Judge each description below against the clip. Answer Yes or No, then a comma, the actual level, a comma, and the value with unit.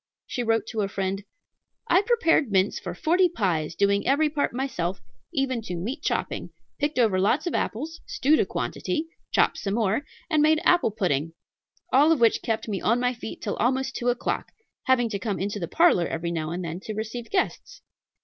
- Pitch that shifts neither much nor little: No, wide, 6.7 semitones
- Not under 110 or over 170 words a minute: No, average, 195 wpm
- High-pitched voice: Yes, high, 230 Hz